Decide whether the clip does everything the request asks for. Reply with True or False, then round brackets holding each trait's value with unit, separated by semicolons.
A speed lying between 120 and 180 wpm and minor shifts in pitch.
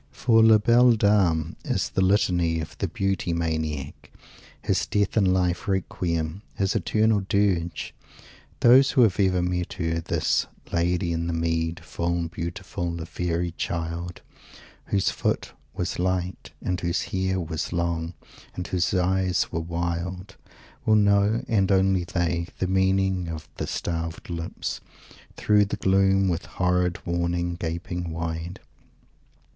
True (140 wpm; 2.3 semitones)